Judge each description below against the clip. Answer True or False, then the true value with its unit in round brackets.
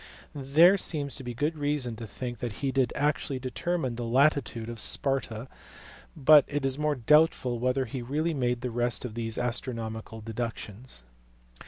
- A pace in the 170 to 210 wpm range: False (155 wpm)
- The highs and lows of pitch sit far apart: False (3.5 semitones)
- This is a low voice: True (130 Hz)